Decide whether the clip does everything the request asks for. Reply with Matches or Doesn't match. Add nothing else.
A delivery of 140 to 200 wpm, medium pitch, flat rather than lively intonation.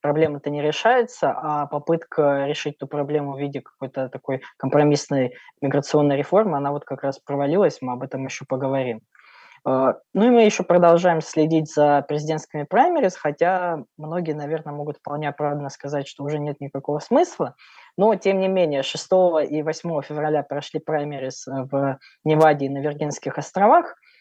Matches